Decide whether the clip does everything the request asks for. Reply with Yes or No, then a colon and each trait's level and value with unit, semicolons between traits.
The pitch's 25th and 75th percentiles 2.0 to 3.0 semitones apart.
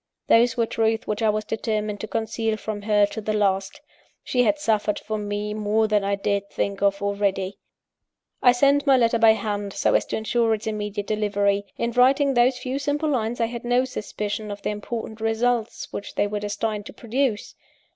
Yes: narrow, 2.5 semitones